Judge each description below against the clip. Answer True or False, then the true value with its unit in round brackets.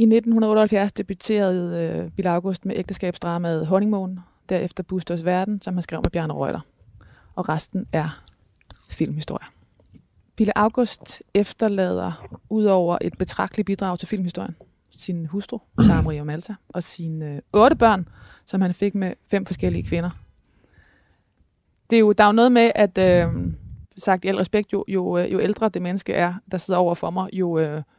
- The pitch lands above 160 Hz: True (185 Hz)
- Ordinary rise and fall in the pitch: True (4.1 semitones)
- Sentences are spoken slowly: False (165 wpm)